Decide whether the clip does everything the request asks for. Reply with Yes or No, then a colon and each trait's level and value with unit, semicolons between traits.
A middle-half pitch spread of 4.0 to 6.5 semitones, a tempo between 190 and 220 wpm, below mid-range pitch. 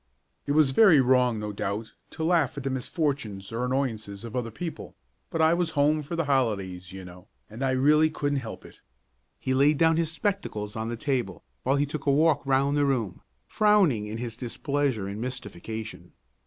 Yes: average, 5.2 semitones; average, 195 wpm; low, 130 Hz